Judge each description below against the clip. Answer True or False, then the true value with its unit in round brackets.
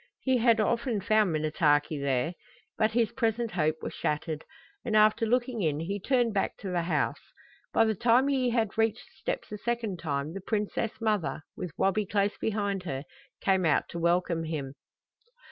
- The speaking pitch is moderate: False (205 Hz)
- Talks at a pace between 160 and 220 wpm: True (180 wpm)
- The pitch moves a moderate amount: False (5.7 semitones)